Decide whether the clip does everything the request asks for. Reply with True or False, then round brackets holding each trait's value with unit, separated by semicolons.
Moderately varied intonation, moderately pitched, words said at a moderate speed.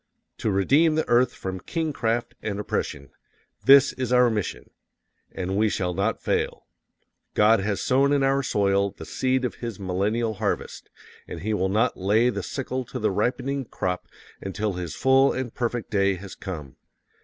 False (4.8 semitones; 110 Hz; 165 wpm)